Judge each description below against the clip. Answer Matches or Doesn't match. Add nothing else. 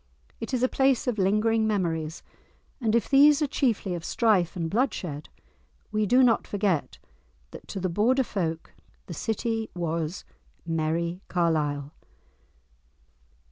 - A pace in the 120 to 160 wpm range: Matches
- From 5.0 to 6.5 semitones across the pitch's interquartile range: Matches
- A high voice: Matches